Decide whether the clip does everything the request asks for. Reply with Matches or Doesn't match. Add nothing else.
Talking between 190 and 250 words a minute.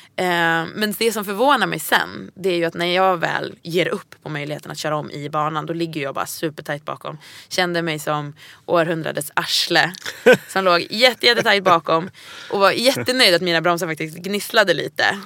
Doesn't match